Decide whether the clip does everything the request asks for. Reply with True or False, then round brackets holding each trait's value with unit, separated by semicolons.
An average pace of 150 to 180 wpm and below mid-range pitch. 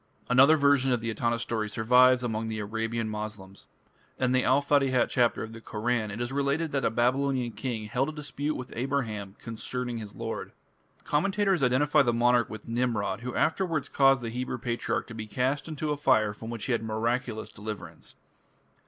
False (190 wpm; 120 Hz)